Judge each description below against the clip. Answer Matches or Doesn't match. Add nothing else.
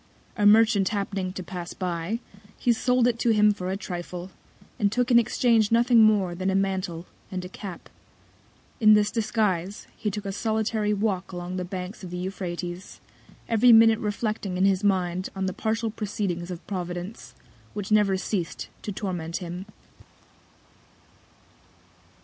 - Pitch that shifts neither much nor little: Matches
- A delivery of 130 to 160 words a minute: Matches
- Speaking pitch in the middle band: Doesn't match